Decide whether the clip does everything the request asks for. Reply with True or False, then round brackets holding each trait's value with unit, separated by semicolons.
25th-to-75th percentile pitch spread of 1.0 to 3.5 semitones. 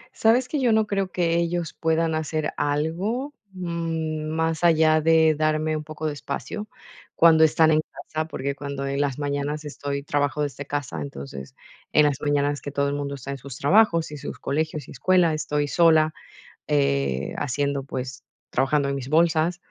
True (2.5 semitones)